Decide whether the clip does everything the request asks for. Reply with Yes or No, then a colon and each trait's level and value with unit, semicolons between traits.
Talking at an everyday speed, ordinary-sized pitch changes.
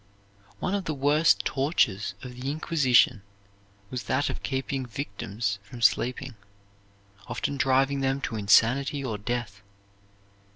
No: slow, 125 wpm; average, 3.4 semitones